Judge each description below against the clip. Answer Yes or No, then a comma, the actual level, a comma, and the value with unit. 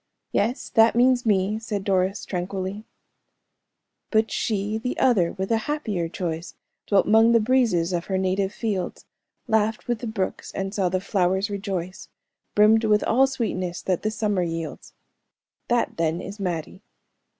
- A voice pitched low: No, high, 200 Hz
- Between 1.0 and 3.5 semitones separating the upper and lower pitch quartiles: Yes, average, 3.1 semitones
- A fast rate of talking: No, average, 155 wpm